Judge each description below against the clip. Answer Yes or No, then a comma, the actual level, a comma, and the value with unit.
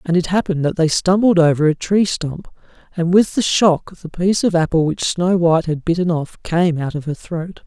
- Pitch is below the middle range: No, medium, 170 Hz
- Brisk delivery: Yes, fast, 225 wpm